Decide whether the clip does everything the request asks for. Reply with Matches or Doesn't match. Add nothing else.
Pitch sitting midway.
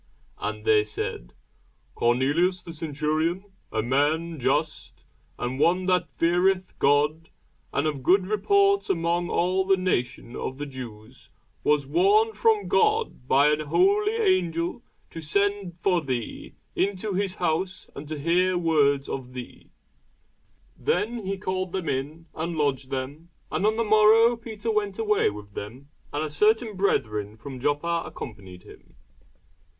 Matches